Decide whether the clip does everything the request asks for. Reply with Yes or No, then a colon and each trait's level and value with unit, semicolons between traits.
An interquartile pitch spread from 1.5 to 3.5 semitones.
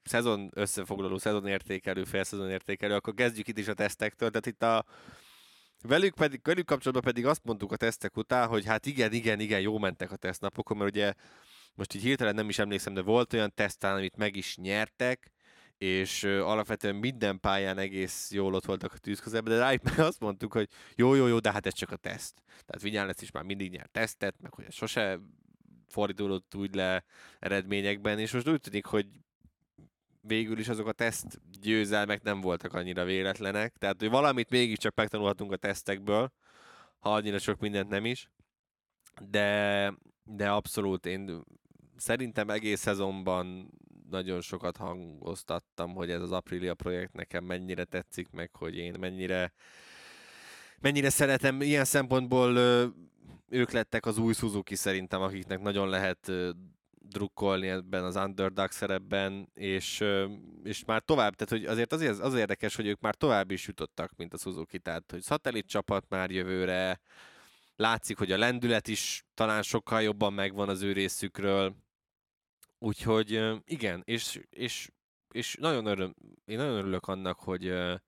Yes: average, 2.9 semitones